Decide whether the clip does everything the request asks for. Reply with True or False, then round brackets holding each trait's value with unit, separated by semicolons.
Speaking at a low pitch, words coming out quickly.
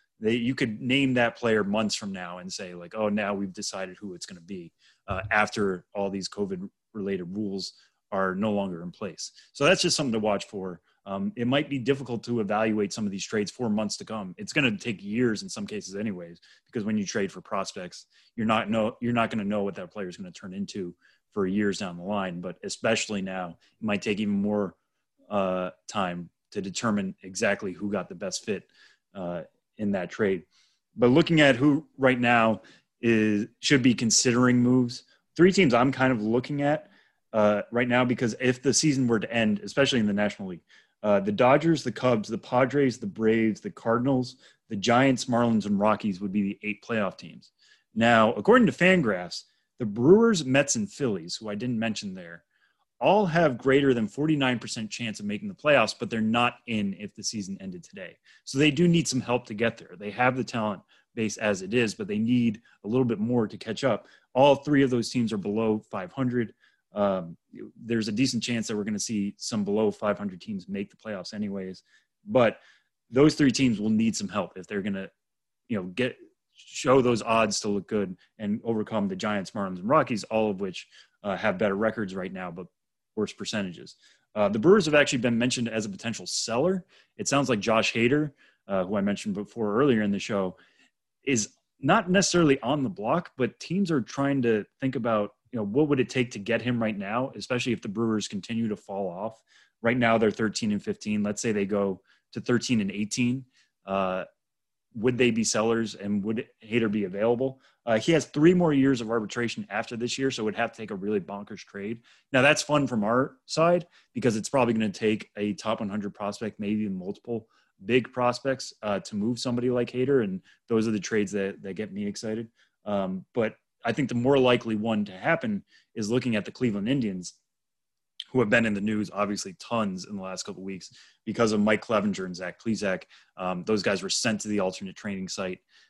True (115 Hz; 210 wpm)